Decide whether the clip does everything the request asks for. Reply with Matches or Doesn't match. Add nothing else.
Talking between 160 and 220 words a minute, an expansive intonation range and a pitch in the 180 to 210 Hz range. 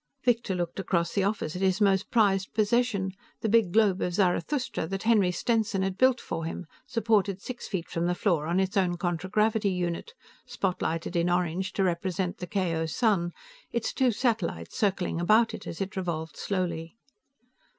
Doesn't match